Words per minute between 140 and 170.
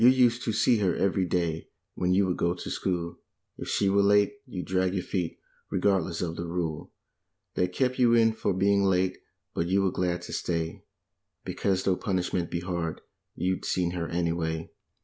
No: average, 190 wpm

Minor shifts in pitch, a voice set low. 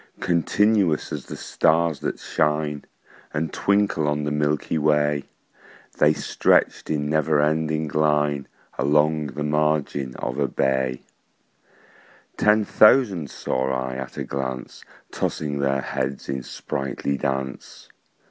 Yes: narrow, 2.3 semitones; very low, 75 Hz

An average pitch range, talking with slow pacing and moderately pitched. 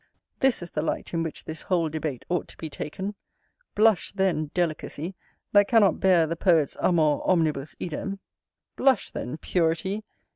No: average, 3.5 semitones; average, 155 wpm; medium, 170 Hz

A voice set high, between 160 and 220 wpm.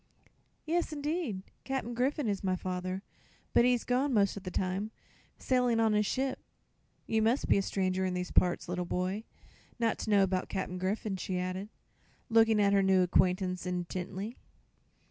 Yes: high, 200 Hz; average, 165 wpm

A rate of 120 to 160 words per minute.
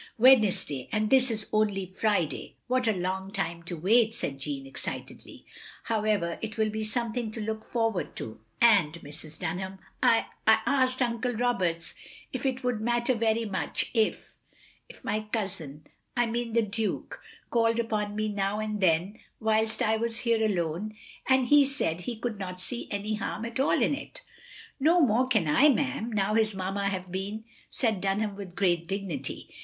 No: average, 185 wpm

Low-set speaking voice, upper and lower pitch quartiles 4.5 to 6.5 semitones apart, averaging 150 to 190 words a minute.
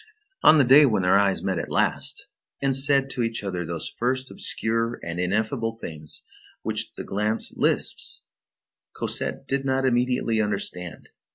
Yes: low, 115 Hz; average, 5.3 semitones; average, 155 wpm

